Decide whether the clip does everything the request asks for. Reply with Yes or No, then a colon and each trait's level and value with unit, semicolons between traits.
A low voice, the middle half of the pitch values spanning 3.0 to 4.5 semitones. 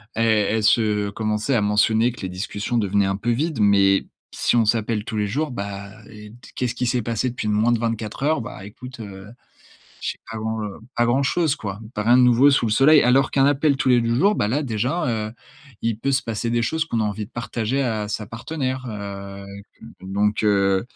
Yes: low, 115 Hz; average, 3.3 semitones